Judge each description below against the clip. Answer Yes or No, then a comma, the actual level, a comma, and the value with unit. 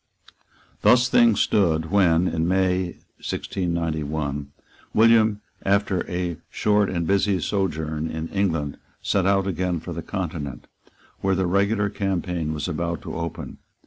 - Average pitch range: Yes, average, 3.5 semitones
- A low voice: Yes, very low, 90 Hz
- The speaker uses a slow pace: Yes, slow, 130 wpm